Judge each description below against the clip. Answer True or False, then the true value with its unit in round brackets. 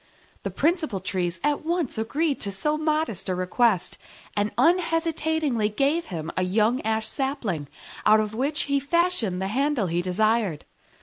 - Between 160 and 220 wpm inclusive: False (150 wpm)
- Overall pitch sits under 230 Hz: False (235 Hz)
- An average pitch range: False (7.8 semitones)